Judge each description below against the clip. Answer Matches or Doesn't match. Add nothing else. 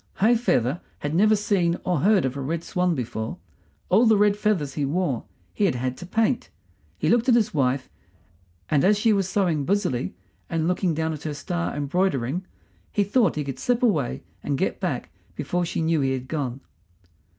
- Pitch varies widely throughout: Matches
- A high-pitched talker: Doesn't match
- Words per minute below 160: Doesn't match